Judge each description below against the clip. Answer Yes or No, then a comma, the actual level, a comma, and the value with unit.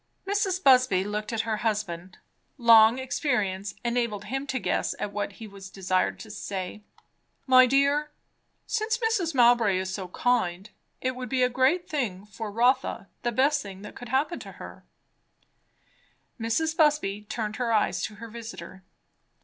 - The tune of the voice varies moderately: Yes, average, 4.5 semitones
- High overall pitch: Yes, high, 230 Hz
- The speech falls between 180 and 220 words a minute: No, average, 160 wpm